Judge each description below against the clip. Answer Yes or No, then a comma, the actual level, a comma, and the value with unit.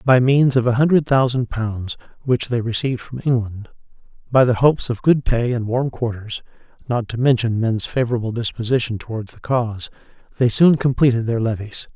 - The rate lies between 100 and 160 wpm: No, average, 175 wpm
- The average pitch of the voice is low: Yes, low, 120 Hz